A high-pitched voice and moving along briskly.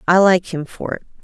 No: medium, 180 Hz; fast, 245 wpm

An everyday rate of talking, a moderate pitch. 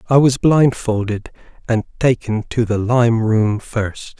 No: average, 145 wpm; low, 115 Hz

